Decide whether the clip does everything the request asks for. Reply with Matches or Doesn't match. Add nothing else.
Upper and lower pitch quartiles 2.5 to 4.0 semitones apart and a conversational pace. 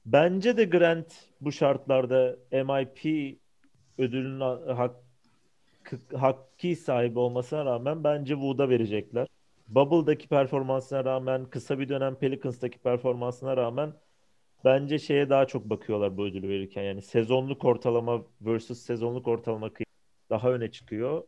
Matches